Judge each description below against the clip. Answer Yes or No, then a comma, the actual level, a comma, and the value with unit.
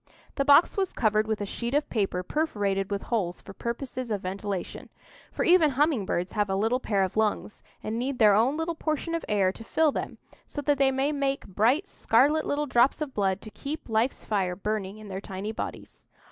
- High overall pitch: Yes, high, 225 Hz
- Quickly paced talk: Yes, fast, 210 wpm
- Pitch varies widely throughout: Yes, wide, 5.8 semitones